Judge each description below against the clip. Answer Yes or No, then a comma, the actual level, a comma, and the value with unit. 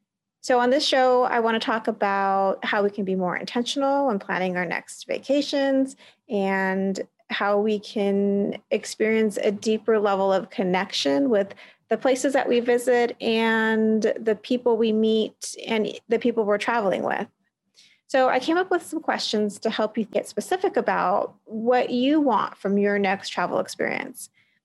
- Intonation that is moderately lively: Yes, average, 3.7 semitones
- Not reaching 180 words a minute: Yes, average, 165 wpm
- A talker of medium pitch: No, high, 225 Hz